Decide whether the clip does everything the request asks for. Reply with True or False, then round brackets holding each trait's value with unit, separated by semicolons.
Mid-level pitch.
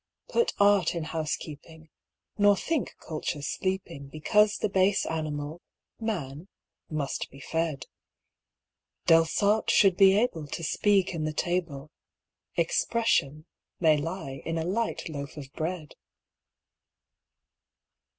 True (165 Hz)